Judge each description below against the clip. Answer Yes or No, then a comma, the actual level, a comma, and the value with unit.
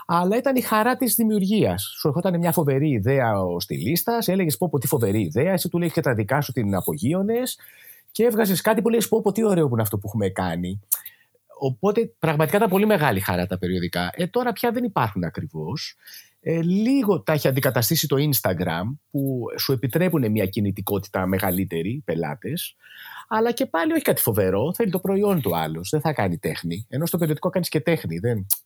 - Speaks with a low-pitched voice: No, medium, 155 Hz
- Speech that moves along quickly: Yes, fast, 195 wpm